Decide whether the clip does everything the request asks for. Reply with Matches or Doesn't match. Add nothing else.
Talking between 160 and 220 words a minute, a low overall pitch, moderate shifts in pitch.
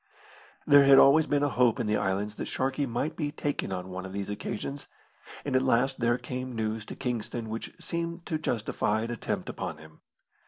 Matches